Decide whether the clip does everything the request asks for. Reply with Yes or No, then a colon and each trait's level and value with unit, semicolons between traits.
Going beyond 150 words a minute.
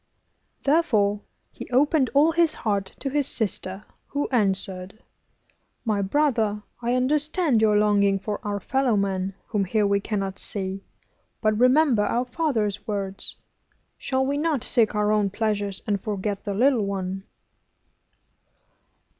No: slow, 135 wpm